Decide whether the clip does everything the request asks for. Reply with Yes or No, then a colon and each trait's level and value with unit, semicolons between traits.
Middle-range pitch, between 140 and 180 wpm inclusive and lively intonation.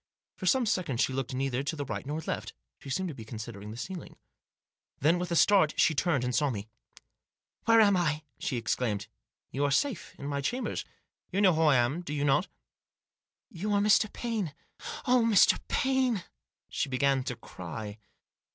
No: medium, 150 Hz; fast, 205 wpm; wide, 7.1 semitones